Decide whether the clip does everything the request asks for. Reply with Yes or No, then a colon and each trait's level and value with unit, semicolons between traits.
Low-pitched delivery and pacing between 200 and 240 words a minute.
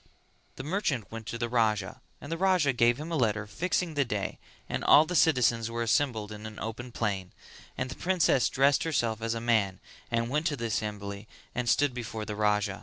Yes: low, 115 Hz; fast, 205 wpm